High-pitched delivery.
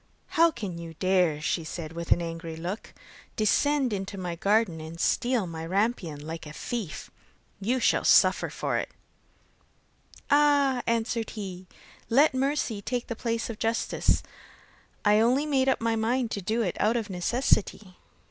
Yes: high, 215 Hz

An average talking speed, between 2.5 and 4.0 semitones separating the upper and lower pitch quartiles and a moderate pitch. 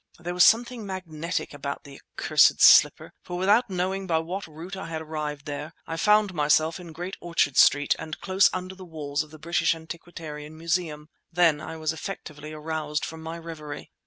Yes: average, 185 wpm; average, 2.9 semitones; medium, 165 Hz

